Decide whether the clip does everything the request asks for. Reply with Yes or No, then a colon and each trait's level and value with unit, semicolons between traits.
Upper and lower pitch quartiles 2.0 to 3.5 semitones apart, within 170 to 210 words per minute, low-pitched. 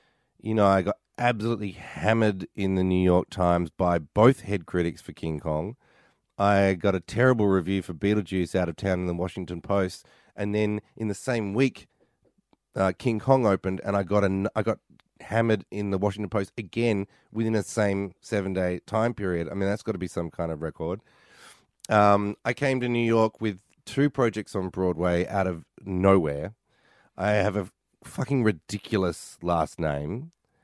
Yes: average, 3.1 semitones; average, 180 wpm; low, 100 Hz